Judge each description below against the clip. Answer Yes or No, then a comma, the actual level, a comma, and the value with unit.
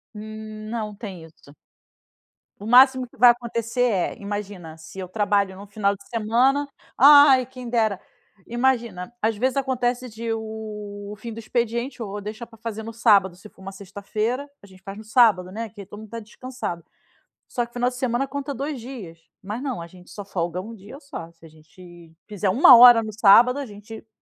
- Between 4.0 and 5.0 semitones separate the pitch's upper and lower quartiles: No, average, 3.4 semitones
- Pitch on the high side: Yes, high, 220 Hz